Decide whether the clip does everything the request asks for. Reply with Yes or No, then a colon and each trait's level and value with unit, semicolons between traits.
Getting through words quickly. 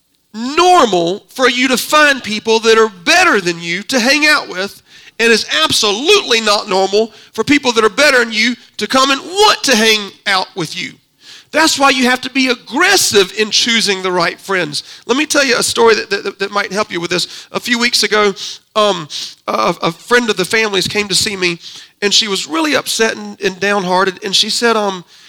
Yes: fast, 210 wpm